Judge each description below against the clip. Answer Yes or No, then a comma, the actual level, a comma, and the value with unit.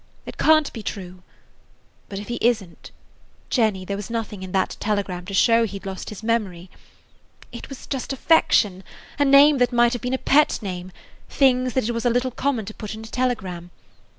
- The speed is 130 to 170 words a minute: No, average, 195 wpm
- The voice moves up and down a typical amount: Yes, average, 4.4 semitones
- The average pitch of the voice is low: No, high, 225 Hz